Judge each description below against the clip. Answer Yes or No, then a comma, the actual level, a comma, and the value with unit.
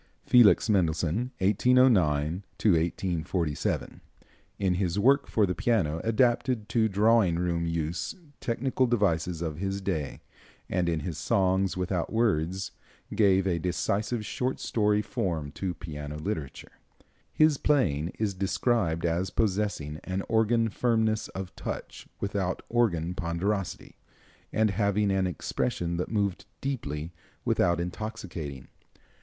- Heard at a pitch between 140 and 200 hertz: No, very low, 95 Hz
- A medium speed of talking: No, slow, 120 wpm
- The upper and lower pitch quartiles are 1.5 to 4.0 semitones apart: No, average, 4.5 semitones